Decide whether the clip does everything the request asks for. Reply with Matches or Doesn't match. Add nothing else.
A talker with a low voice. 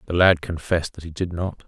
Matches